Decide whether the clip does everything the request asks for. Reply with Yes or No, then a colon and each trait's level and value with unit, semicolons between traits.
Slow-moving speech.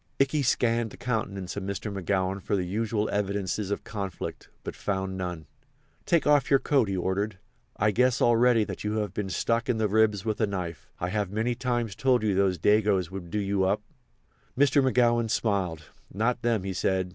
No: average, 190 wpm